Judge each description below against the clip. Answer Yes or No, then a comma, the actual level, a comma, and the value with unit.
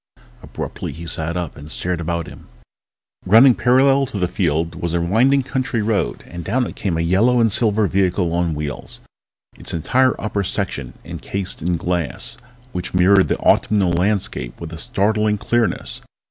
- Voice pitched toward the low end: Yes, very low, 95 Hz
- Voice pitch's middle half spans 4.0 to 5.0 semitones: Yes, average, 4.5 semitones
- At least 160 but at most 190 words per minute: Yes, average, 165 wpm